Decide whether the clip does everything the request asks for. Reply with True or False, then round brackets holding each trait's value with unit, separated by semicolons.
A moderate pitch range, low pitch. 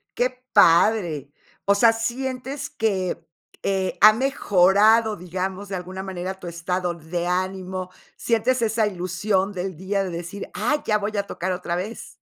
False (3.4 semitones; 190 Hz)